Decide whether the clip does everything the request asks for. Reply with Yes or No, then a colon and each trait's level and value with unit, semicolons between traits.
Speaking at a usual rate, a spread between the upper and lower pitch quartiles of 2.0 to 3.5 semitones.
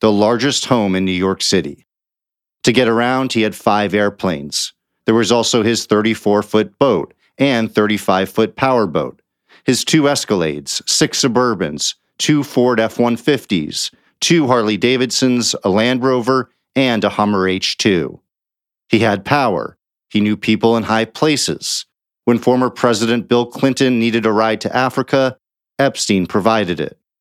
Yes: average, 150 wpm; average, 3.2 semitones